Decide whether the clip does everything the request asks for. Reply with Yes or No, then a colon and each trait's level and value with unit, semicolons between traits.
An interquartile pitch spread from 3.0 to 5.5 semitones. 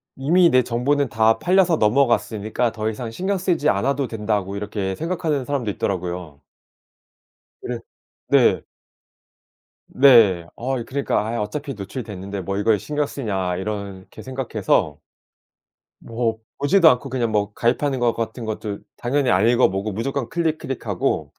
Yes: average, 5.1 semitones